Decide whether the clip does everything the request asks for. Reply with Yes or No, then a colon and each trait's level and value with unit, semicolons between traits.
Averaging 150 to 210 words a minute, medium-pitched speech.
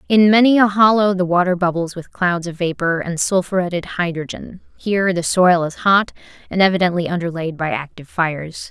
Yes: average, 170 wpm; medium, 180 Hz